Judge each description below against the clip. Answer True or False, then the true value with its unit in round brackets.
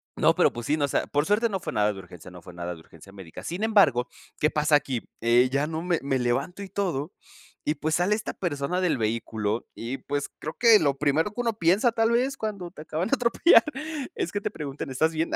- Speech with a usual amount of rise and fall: False (7.9 semitones)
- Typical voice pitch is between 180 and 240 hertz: False (150 Hz)